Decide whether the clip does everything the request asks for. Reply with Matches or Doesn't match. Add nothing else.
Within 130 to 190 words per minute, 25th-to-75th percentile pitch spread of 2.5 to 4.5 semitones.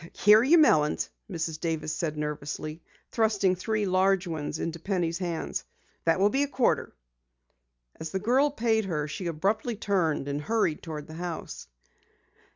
Doesn't match